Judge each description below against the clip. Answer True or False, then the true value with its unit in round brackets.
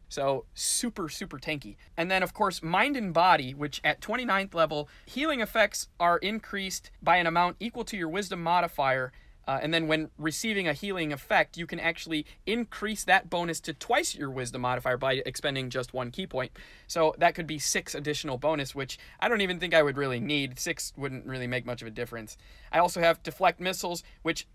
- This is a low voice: False (165 Hz)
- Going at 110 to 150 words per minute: False (200 wpm)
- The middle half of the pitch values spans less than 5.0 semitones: False (5.3 semitones)